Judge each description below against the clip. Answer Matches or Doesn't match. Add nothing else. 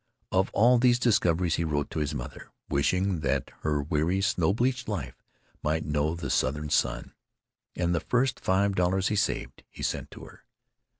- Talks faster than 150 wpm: Matches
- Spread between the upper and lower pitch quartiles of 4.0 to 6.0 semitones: Matches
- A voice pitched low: Matches